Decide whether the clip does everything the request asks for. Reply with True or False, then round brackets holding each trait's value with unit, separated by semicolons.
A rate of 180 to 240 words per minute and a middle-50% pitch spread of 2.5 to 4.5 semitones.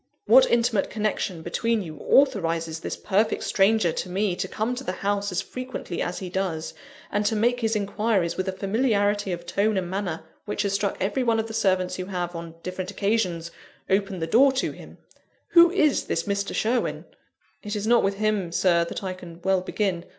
True (200 wpm; 3.3 semitones)